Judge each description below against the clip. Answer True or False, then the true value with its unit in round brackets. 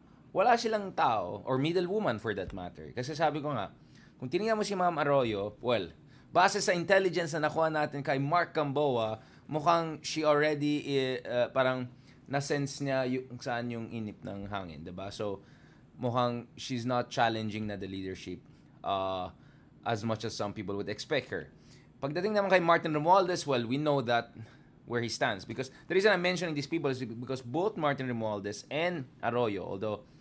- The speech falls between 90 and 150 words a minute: False (175 wpm)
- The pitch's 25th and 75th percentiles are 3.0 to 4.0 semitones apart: False (5.6 semitones)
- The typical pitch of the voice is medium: False (130 Hz)